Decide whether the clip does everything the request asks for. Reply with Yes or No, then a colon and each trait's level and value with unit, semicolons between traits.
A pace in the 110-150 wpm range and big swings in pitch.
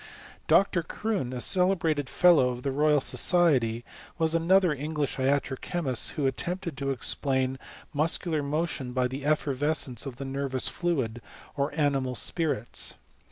No: average, 145 wpm; average, 3.9 semitones